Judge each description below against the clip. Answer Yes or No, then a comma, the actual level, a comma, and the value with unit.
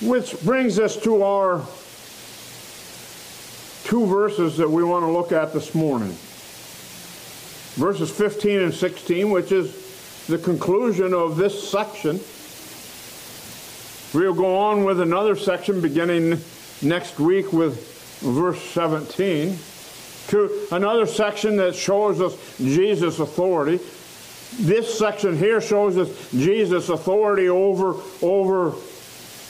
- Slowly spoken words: Yes, slow, 110 wpm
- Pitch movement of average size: Yes, average, 3.3 semitones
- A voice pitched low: No, medium, 185 Hz